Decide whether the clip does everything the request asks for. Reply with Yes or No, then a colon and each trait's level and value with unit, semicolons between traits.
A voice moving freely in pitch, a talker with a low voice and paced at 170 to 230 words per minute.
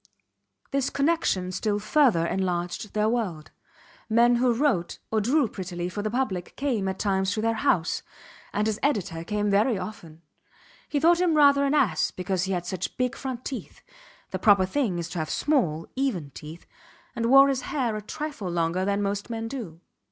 No: wide, 6.1 semitones; high, 210 Hz; average, 180 wpm